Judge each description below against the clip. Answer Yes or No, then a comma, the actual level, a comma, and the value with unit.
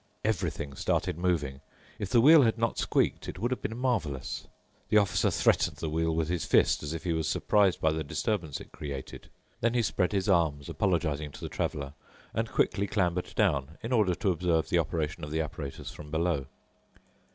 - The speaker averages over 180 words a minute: Yes, average, 195 wpm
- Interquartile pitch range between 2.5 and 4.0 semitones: No, average, 5.0 semitones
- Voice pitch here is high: No, very low, 85 Hz